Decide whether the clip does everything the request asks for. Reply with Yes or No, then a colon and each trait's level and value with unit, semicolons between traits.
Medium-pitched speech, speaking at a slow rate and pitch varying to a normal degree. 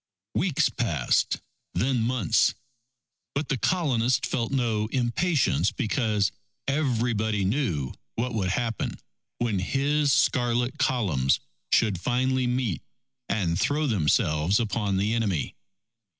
No: low, 115 Hz; slow, 105 wpm; average, 4.4 semitones